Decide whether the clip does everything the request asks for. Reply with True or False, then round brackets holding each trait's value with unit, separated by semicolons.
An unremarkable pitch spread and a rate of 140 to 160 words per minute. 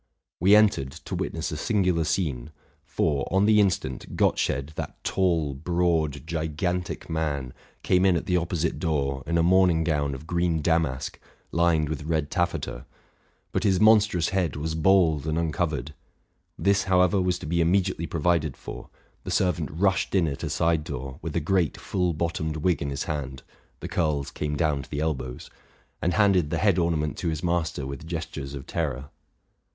False (3.3 semitones; 175 wpm)